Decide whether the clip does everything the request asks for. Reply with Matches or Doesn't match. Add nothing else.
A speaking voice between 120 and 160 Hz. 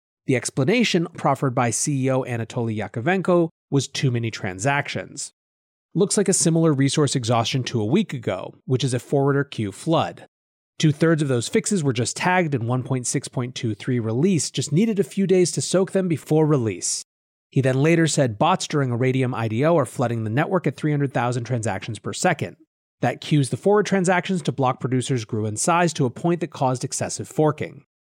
Matches